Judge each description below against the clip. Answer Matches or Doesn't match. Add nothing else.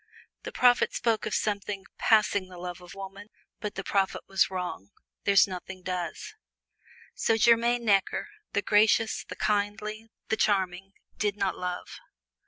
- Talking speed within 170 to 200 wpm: Doesn't match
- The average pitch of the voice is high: Matches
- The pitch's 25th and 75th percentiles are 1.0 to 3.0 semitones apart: Matches